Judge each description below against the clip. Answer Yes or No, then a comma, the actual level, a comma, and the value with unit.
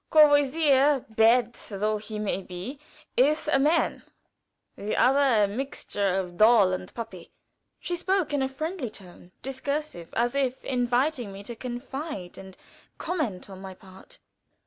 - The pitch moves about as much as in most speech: No, wide, 6.1 semitones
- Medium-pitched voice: No, high, 245 Hz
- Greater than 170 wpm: No, slow, 135 wpm